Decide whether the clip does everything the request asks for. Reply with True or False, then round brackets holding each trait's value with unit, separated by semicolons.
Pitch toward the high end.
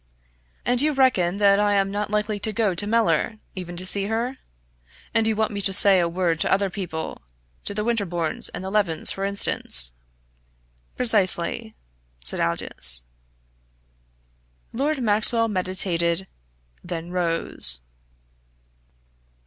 True (200 Hz)